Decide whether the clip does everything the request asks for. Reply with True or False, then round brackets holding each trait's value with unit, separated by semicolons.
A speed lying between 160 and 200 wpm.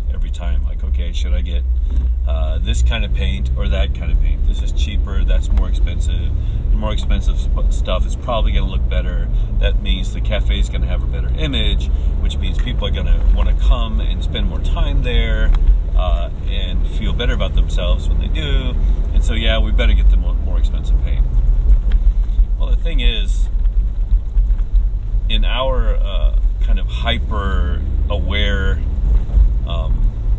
True (170 wpm)